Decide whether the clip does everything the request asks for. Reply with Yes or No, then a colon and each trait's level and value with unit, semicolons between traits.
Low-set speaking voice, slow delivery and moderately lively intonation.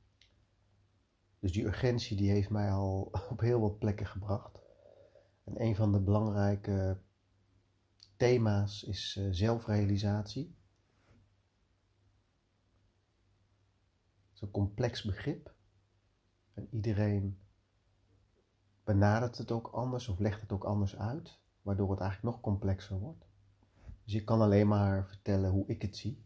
No: low, 100 Hz; slow, 120 wpm; narrow, 1.6 semitones